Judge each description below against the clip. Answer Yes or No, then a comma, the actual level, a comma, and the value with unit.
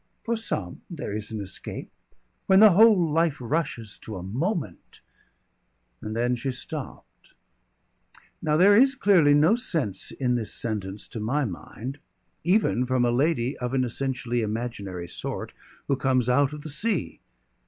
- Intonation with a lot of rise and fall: Yes, wide, 6.5 semitones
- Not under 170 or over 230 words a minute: No, average, 155 wpm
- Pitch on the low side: Yes, low, 130 Hz